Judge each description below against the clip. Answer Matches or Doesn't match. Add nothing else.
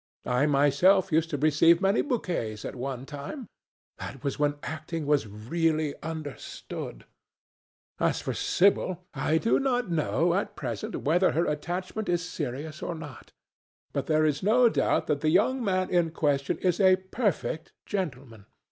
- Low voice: Doesn't match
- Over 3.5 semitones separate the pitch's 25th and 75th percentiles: Matches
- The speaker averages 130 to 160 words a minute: Matches